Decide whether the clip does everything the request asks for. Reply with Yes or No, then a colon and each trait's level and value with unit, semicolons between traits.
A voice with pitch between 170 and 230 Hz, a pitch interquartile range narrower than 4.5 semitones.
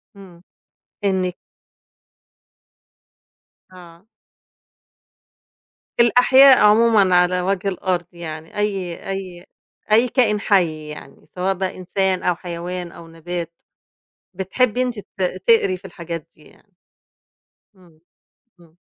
Yes: medium, 185 Hz; average, 2.7 semitones